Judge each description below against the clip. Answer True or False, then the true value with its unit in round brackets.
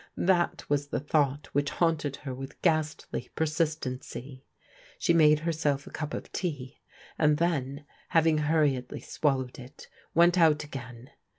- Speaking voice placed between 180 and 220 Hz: False (150 Hz)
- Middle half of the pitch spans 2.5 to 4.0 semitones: True (2.9 semitones)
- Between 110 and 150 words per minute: True (140 wpm)